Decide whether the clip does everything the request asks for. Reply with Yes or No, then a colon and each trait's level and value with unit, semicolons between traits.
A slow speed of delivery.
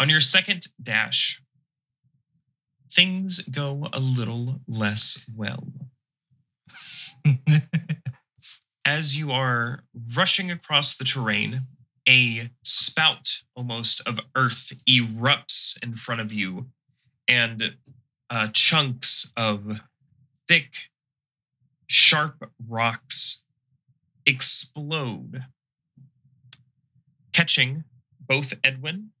Yes: slow, 80 wpm